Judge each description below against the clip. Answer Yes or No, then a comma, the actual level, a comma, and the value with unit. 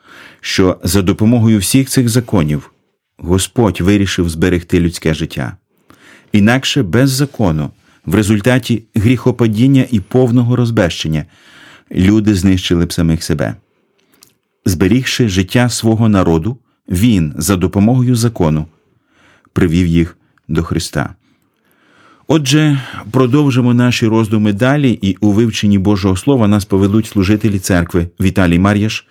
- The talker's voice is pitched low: Yes, low, 105 Hz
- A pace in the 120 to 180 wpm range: No, average, 110 wpm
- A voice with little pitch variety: No, average, 5.0 semitones